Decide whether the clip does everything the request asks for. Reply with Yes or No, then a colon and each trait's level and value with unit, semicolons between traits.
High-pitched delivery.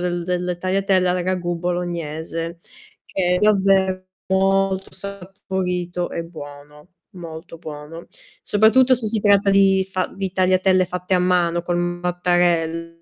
No: medium, 180 Hz